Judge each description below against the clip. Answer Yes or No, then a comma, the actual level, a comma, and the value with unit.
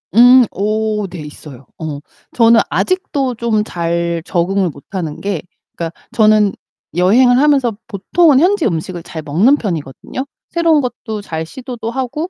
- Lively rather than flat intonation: Yes, wide, 6.9 semitones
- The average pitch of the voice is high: Yes, high, 215 Hz